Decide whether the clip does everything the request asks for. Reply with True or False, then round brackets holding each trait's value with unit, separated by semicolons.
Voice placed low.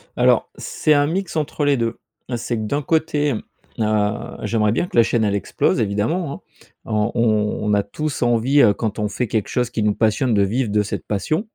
True (115 Hz)